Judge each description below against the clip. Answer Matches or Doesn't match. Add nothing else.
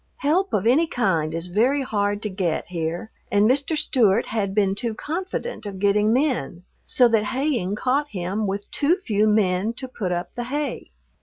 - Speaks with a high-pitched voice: Matches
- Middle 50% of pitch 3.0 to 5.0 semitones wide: Doesn't match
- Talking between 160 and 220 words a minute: Matches